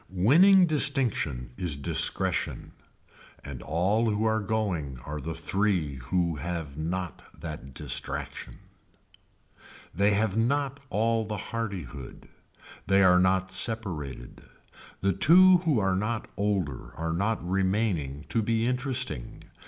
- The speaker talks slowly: Yes, slow, 120 wpm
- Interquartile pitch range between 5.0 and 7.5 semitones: Yes, wide, 5.6 semitones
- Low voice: Yes, very low, 95 Hz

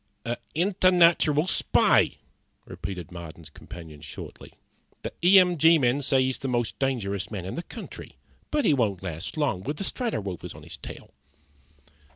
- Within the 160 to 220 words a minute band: Yes, average, 165 wpm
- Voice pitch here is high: No, low, 130 Hz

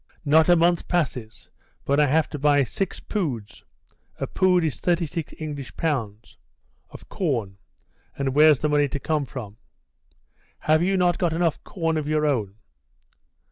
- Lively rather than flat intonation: No, average, 3.4 semitones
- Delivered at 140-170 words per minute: Yes, average, 155 wpm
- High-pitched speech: No, medium, 150 Hz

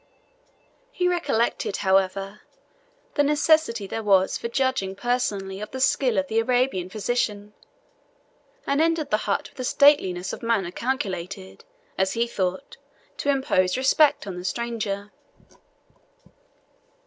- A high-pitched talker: Yes, high, 225 Hz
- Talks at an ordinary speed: No, slow, 125 wpm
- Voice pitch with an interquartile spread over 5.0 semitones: Yes, wide, 5.4 semitones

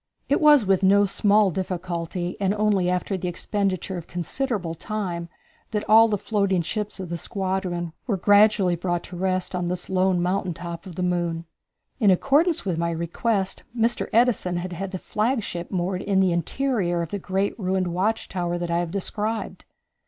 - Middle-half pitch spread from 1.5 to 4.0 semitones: Yes, average, 2.9 semitones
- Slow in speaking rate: No, average, 175 wpm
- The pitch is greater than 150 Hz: Yes, medium, 185 Hz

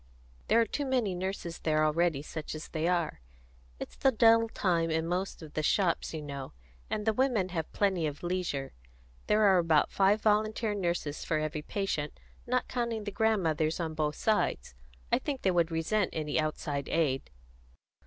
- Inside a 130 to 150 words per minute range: No, average, 175 wpm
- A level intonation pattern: No, average, 5.2 semitones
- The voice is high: No, medium, 175 Hz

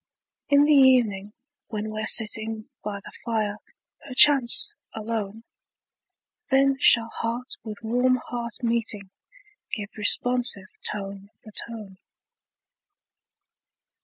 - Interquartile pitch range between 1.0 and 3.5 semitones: Yes, average, 2.9 semitones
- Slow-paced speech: Yes, slow, 100 wpm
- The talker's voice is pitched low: No, high, 225 Hz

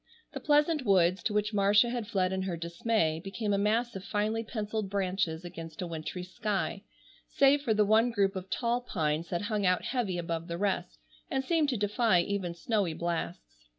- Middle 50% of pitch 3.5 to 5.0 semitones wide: Yes, average, 4.3 semitones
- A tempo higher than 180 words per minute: Yes, average, 190 wpm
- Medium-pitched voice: No, high, 200 Hz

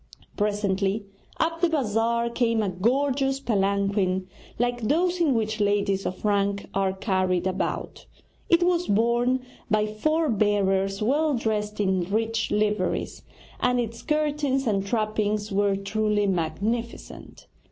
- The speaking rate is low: Yes, slow, 125 wpm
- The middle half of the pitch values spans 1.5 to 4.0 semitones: Yes, average, 3.7 semitones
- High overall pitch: Yes, high, 215 Hz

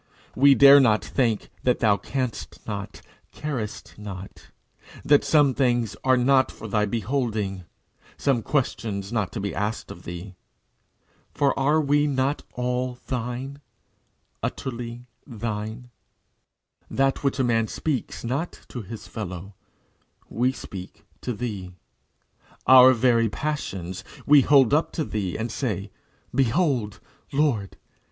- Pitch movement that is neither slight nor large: Yes, average, 4.4 semitones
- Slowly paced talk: Yes, slow, 125 wpm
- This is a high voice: No, low, 120 Hz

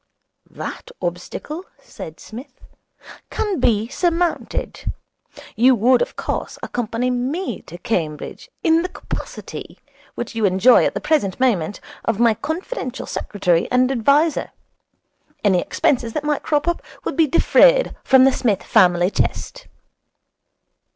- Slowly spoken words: Yes, slow, 130 wpm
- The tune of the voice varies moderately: No, wide, 6.6 semitones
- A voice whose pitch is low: No, very high, 250 Hz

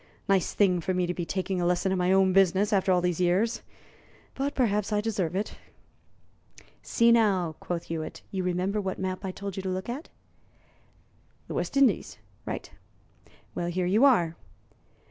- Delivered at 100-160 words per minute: No, average, 175 wpm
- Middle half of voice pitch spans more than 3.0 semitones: No, narrow, 2.6 semitones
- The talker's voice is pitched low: No, high, 190 Hz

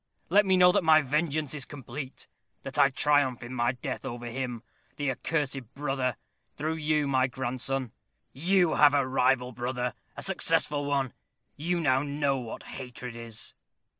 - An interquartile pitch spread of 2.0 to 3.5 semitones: Yes, average, 2.9 semitones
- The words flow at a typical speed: Yes, average, 160 wpm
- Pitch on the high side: No, low, 135 Hz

